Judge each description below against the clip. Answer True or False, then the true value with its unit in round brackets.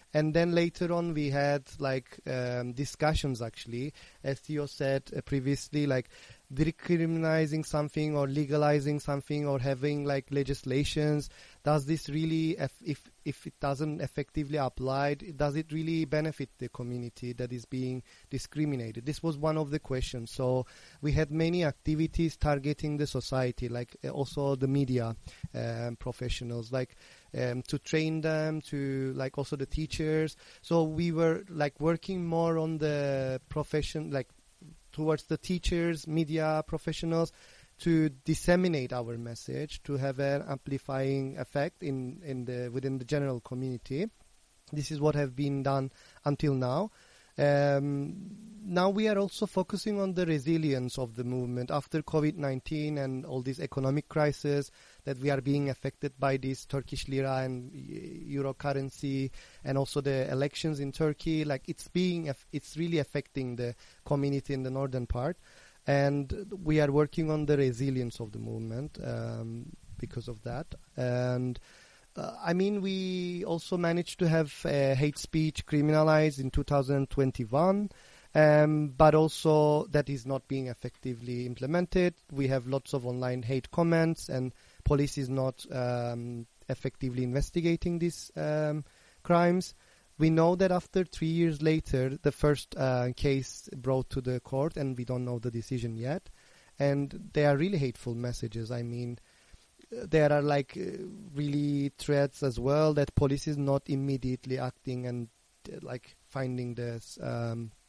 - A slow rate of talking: False (150 wpm)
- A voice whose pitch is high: False (140 Hz)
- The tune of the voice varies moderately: True (3.2 semitones)